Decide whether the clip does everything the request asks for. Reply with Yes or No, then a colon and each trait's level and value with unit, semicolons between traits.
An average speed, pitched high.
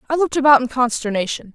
Yes: average, 195 wpm; very high, 255 Hz